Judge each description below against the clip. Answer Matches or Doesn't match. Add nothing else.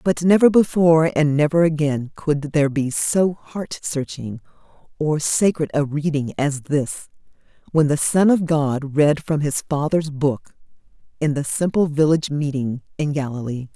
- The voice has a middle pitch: Matches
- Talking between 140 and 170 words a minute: Matches